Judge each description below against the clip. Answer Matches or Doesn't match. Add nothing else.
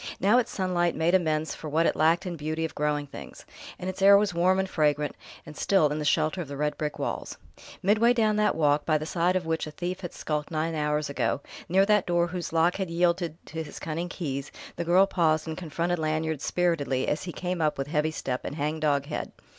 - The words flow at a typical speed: Doesn't match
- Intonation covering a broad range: Doesn't match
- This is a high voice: Doesn't match